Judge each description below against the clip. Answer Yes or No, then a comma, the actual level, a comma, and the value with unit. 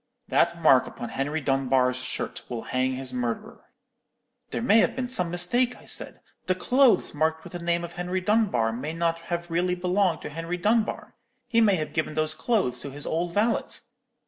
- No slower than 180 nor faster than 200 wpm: Yes, average, 190 wpm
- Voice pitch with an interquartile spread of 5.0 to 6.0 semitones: Yes, wide, 5.4 semitones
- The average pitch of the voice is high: No, medium, 170 Hz